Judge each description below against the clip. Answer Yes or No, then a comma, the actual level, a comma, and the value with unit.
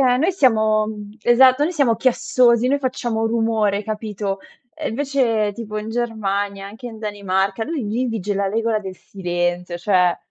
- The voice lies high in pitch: Yes, high, 220 Hz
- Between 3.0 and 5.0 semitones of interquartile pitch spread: Yes, average, 3.3 semitones